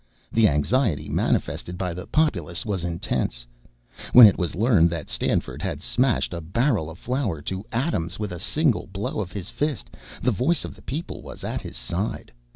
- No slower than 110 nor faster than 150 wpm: No, average, 180 wpm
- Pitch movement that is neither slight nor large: No, wide, 6.6 semitones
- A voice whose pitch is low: Yes, low, 100 Hz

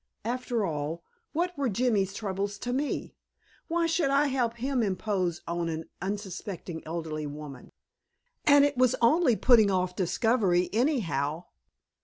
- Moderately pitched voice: No, high, 205 Hz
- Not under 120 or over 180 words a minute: Yes, slow, 135 wpm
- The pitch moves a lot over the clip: Yes, wide, 6.6 semitones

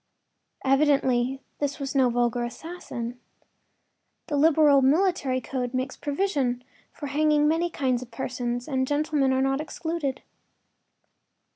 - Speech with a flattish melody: No, average, 3.1 semitones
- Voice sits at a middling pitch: No, very high, 270 Hz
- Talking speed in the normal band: No, slow, 120 wpm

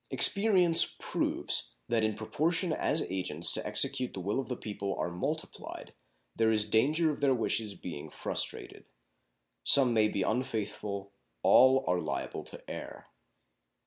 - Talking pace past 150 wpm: No, average, 145 wpm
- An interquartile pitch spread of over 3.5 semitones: Yes, average, 5.3 semitones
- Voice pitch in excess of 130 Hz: No, low, 110 Hz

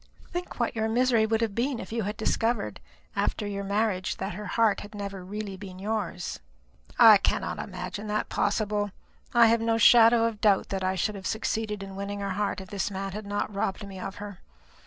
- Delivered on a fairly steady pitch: Yes, narrow, 2.2 semitones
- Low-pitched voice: No, high, 205 Hz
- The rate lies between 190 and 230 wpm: Yes, fast, 205 wpm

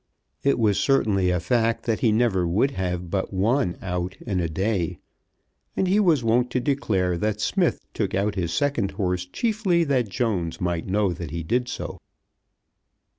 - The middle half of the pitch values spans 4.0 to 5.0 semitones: No, wide, 5.4 semitones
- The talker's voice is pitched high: No, low, 100 Hz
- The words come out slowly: No, average, 175 wpm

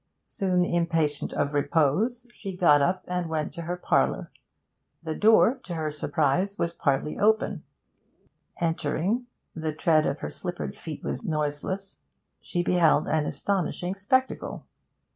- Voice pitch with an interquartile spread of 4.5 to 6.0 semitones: No, average, 3.8 semitones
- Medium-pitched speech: Yes, medium, 170 Hz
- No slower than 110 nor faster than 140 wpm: Yes, slow, 135 wpm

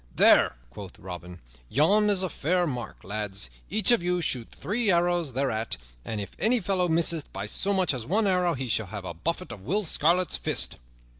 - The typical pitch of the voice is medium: Yes, medium, 165 Hz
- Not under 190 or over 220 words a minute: Yes, average, 195 wpm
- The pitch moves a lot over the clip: Yes, wide, 9.0 semitones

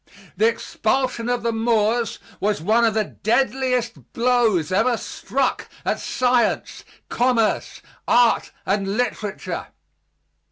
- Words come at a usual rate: No, slow, 110 wpm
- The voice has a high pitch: Yes, high, 230 Hz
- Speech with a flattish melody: Yes, narrow, 2.3 semitones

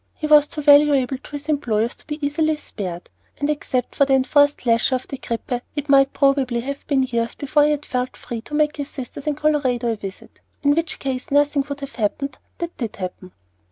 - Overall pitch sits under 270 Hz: No, very high, 275 Hz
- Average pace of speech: No, fast, 210 wpm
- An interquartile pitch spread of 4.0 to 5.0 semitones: No, average, 3.1 semitones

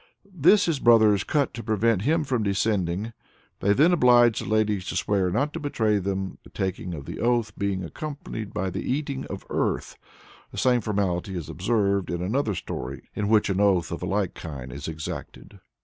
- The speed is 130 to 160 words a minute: No, average, 190 wpm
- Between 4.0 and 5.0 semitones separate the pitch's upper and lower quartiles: Yes, average, 4.5 semitones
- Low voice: Yes, low, 105 Hz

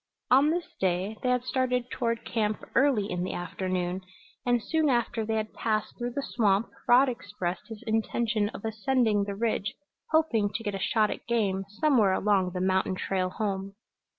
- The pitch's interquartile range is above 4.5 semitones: No, average, 3.7 semitones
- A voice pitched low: No, high, 220 Hz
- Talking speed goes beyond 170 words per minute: Yes, average, 180 wpm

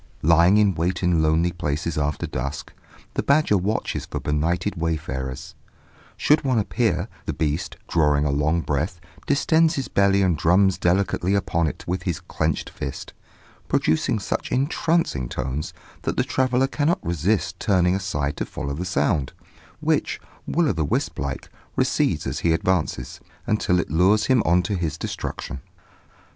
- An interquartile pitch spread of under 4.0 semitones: No, average, 4.8 semitones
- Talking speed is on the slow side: No, average, 155 wpm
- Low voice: Yes, very low, 85 Hz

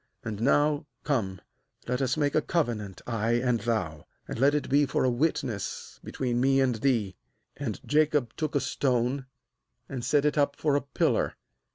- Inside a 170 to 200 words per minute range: Yes, average, 180 wpm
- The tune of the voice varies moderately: Yes, average, 3.7 semitones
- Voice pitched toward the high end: No, low, 130 Hz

